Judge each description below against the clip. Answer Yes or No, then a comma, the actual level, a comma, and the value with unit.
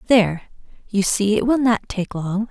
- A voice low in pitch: No, high, 210 Hz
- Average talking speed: Yes, average, 190 wpm